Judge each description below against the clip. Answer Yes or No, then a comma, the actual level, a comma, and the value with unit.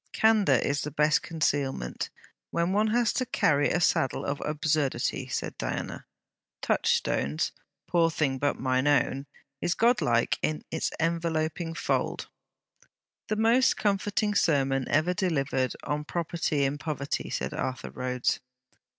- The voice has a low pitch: No, medium, 155 Hz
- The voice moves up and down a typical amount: Yes, average, 4.1 semitones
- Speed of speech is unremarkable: No, slow, 130 wpm